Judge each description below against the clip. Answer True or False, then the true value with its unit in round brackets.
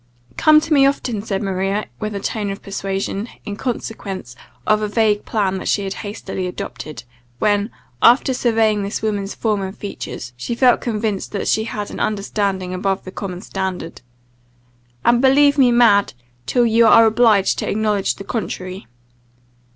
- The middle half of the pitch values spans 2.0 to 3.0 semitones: True (2.7 semitones)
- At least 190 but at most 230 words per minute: False (165 wpm)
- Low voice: False (210 Hz)